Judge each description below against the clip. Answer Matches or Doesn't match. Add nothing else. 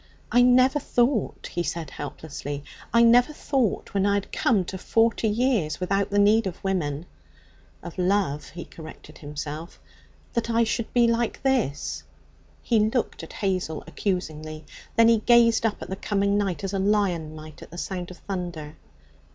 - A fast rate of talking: Doesn't match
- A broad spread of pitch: Matches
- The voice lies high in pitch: Matches